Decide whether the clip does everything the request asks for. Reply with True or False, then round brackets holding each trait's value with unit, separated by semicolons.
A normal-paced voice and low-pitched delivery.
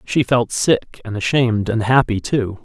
True (180 wpm; 115 Hz)